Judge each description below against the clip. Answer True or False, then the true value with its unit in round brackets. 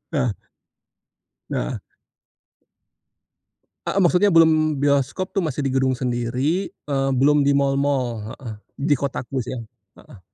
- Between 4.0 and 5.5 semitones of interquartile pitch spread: False (3.1 semitones)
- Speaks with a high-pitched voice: False (140 Hz)